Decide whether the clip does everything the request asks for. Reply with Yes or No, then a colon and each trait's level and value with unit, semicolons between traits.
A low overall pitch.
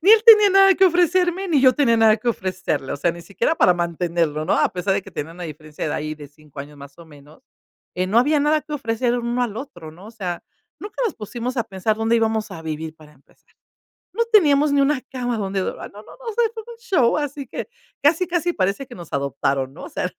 No: high, 225 Hz